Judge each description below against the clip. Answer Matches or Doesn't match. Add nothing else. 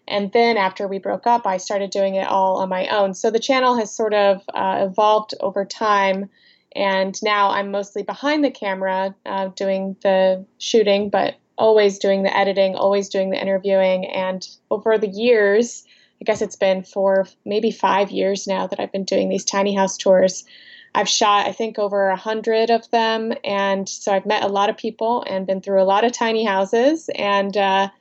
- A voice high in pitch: Matches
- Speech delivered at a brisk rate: Doesn't match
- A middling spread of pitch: Doesn't match